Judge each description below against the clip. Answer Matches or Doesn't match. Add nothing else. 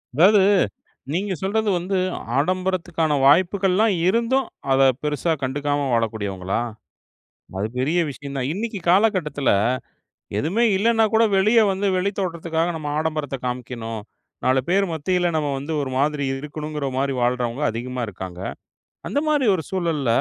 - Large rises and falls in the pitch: Matches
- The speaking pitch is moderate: Matches